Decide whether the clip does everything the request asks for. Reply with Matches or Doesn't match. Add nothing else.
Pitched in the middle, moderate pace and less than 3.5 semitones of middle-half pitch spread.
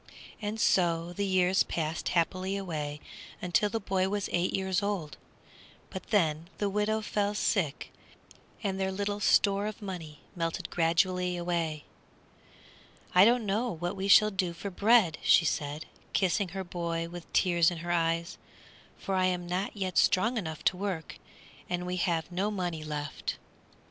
Matches